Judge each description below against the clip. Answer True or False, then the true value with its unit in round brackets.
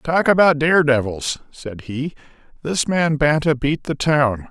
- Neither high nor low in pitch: True (145 Hz)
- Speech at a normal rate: True (145 wpm)